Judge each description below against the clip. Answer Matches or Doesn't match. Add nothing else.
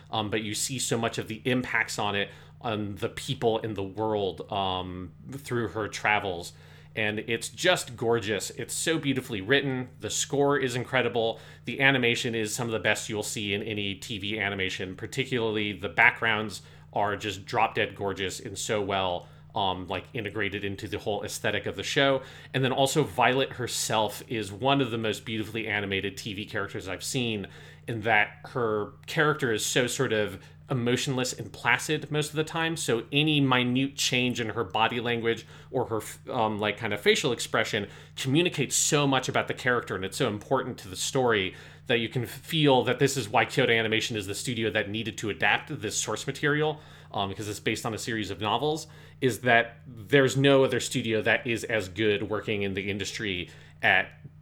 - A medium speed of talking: Matches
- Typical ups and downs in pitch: Matches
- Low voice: Matches